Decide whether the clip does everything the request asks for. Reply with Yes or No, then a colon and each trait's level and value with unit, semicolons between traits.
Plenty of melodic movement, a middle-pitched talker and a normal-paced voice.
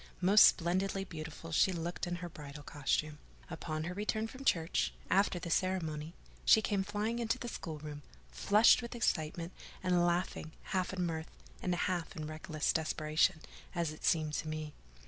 No: average, 3.5 semitones; medium, 170 Hz; average, 165 wpm